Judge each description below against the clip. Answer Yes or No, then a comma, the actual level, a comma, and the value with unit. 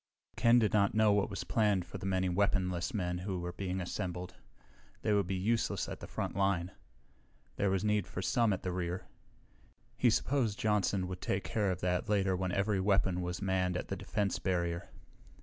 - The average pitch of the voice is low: Yes, very low, 95 Hz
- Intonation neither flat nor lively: No, narrow, 2.3 semitones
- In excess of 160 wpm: Yes, average, 190 wpm